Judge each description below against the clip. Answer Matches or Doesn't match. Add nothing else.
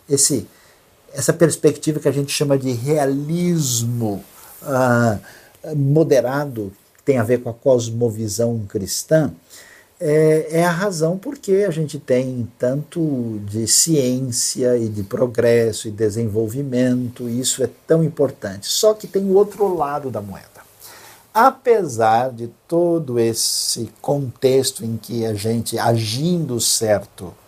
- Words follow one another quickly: Doesn't match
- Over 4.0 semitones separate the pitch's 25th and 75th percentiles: Matches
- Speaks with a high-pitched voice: Doesn't match